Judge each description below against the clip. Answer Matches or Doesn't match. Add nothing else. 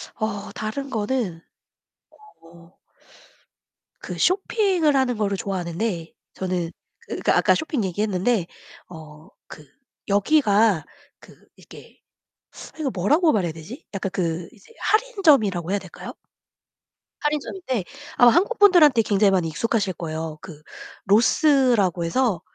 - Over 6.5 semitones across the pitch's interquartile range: Matches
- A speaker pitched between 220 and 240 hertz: Doesn't match